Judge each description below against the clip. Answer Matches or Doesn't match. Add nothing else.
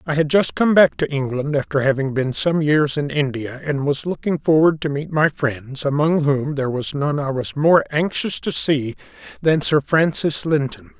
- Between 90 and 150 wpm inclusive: Doesn't match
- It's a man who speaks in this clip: Matches